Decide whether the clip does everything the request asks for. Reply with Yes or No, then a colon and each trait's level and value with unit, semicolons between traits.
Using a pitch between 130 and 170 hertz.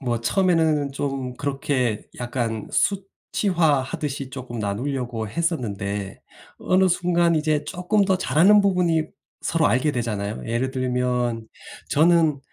Yes: medium, 140 Hz